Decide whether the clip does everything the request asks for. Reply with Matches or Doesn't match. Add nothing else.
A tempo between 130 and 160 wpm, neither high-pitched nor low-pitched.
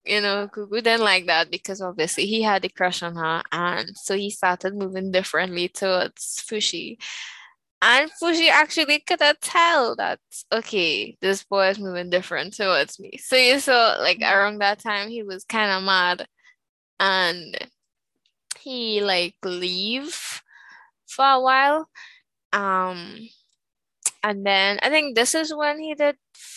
Doesn't match